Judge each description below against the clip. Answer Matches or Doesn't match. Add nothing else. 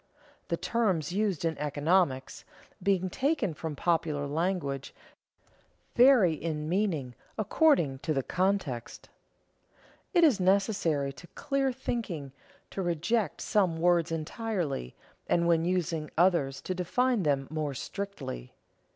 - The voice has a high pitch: Doesn't match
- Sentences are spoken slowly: Matches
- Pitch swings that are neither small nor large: Matches